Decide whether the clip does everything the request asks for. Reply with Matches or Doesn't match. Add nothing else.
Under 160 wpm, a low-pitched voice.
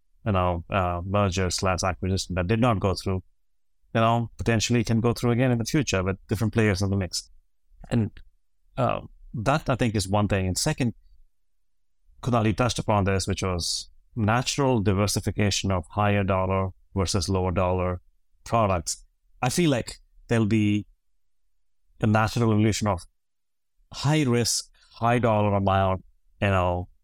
Matches